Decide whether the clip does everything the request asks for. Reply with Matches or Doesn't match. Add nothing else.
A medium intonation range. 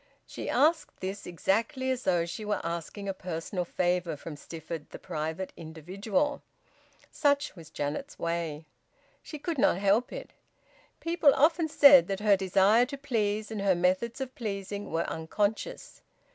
Doesn't match